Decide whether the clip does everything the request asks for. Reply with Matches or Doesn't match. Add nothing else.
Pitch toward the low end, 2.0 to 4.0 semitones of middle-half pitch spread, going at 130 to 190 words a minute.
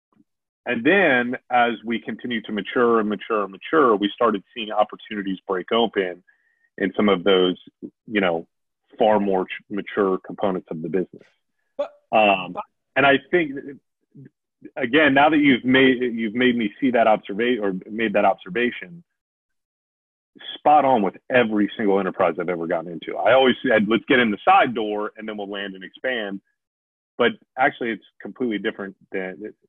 Doesn't match